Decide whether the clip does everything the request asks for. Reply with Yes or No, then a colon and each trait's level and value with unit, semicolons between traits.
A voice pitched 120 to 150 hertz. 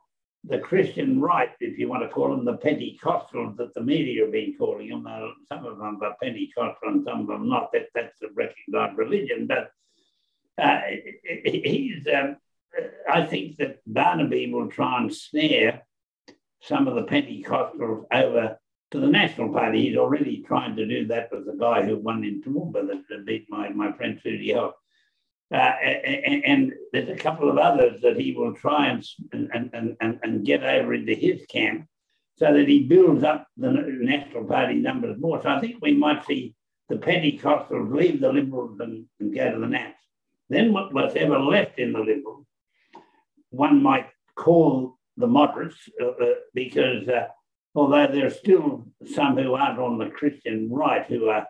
No: very high, 270 Hz